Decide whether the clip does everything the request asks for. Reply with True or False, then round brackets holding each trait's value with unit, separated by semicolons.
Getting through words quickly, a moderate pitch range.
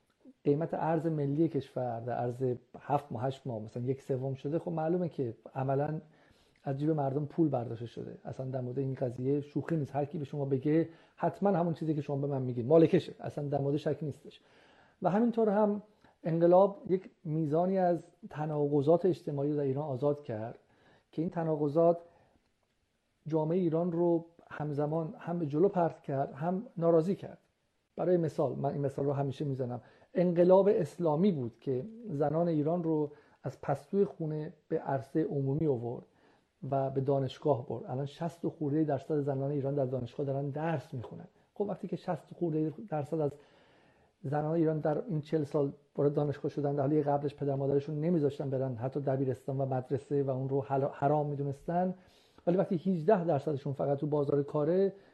True (170 wpm; 3.3 semitones)